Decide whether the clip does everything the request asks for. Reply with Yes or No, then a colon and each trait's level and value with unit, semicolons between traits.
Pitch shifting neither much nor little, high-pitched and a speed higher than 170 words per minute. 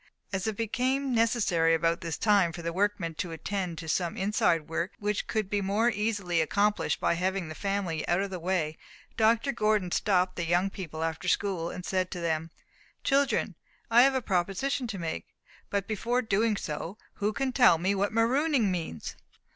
Yes: average, 4.4 semitones; high, 195 Hz; average, 185 wpm